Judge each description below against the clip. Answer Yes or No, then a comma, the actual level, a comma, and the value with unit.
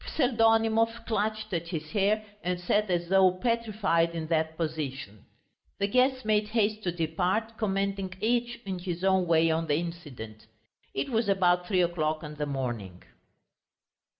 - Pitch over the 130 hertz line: Yes, medium, 185 Hz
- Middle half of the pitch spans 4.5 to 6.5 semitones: Yes, average, 4.9 semitones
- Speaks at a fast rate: No, average, 150 wpm